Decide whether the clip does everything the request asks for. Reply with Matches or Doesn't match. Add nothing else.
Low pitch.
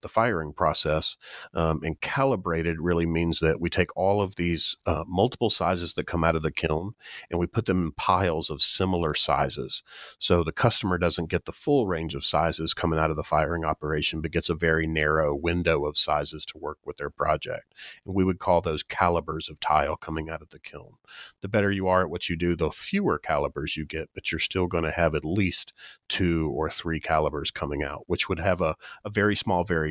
Matches